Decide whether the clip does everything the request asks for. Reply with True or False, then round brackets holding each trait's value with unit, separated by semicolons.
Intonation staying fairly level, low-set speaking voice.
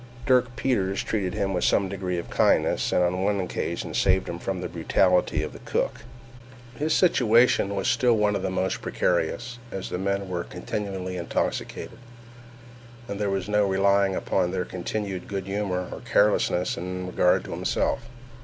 True (2.1 semitones; 95 Hz)